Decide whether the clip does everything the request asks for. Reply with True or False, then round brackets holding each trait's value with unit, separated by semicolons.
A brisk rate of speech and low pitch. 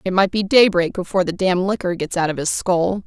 False (255 wpm; 185 Hz)